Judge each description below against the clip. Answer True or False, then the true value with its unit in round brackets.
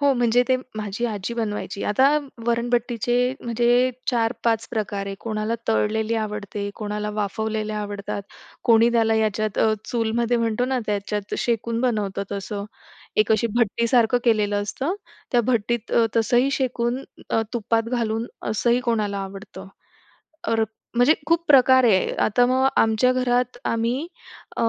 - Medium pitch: False (230 Hz)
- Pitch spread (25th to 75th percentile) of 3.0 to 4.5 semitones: False (2.4 semitones)